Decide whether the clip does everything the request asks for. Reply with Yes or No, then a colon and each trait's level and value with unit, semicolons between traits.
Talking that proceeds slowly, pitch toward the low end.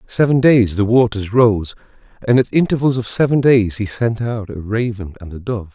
No: average, 200 wpm; low, 110 Hz